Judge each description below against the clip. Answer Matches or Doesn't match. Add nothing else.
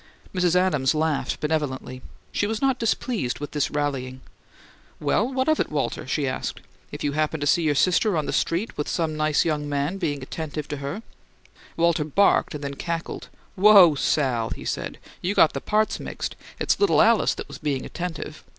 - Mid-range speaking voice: Matches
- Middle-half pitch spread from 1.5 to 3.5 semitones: Doesn't match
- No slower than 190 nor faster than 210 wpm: Matches